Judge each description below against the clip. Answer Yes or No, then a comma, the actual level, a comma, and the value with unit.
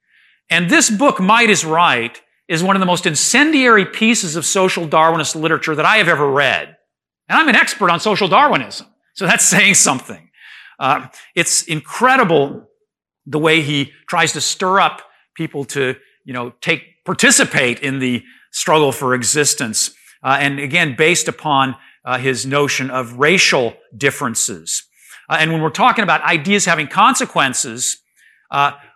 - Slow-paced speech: No, average, 155 wpm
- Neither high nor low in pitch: Yes, medium, 160 Hz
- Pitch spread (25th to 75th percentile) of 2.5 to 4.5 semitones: No, average, 5.1 semitones